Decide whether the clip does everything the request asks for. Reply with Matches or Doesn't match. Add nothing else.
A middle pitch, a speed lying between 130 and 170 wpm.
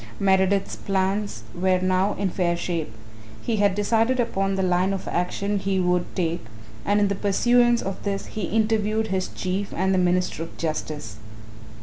Doesn't match